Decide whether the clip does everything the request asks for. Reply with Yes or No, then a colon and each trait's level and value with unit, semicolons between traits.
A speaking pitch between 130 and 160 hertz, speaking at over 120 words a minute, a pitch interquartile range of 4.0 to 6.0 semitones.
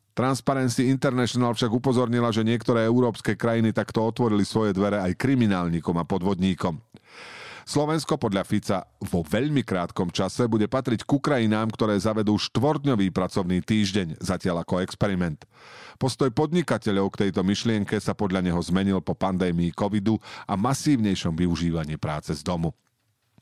No: low, 110 Hz; average, 135 wpm; average, 4.5 semitones